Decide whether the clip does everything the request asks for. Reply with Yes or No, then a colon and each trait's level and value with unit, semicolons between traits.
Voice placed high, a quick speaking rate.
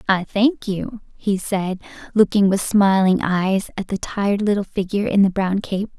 No: high, 195 Hz; average, 180 wpm